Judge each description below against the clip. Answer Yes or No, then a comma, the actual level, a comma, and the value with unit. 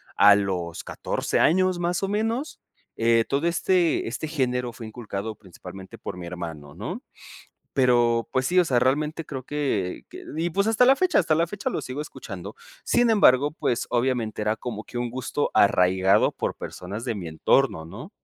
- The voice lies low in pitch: Yes, low, 125 Hz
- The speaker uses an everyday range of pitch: No, wide, 8.2 semitones